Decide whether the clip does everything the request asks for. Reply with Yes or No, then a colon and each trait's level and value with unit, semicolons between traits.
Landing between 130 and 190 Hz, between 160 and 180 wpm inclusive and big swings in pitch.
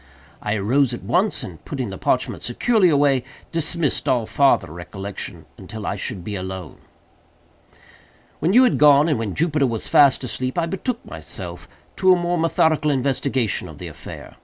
Yes: medium, 140 Hz; average, 165 wpm; wide, 7.1 semitones